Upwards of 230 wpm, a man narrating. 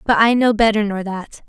No: fast, 245 wpm; female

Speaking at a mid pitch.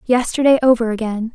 No: high, 240 Hz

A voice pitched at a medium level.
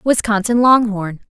No: high, 220 Hz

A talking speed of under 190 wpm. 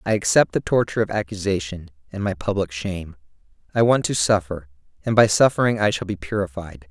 Yes: average, 180 wpm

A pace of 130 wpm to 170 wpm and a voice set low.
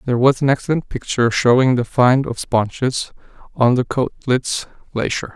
Yes: average, 155 wpm; low, 125 Hz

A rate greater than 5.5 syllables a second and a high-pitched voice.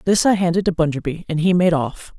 No: 6.0 syllables/s; medium, 170 Hz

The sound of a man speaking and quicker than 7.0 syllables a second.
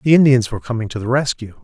Yes: male; 7.3 syllables/s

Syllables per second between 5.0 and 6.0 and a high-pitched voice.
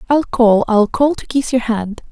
No: 4.3 syllables/s; high, 240 Hz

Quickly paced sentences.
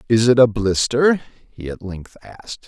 No: average, 180 wpm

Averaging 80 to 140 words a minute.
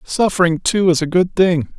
No: average, 200 wpm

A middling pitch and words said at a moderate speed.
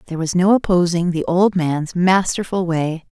Yes: medium, 175 Hz; average, 170 wpm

